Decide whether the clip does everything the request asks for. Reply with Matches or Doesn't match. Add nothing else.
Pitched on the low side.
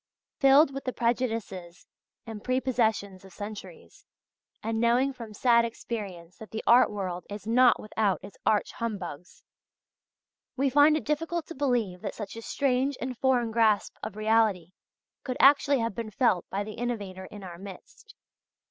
Doesn't match